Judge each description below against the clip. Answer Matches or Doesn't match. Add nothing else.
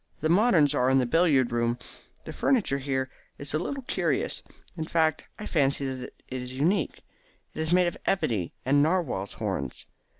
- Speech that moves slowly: Doesn't match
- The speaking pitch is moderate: Matches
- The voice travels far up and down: Doesn't match